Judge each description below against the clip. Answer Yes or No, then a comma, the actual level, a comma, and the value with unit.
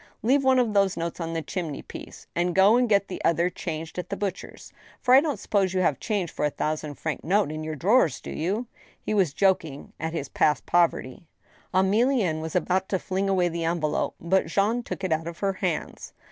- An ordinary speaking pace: No, fast, 220 wpm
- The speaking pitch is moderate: Yes, medium, 180 Hz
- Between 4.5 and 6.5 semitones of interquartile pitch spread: No, average, 3.7 semitones